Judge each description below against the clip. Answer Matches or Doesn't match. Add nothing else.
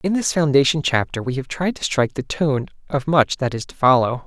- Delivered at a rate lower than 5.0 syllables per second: Doesn't match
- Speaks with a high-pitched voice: Doesn't match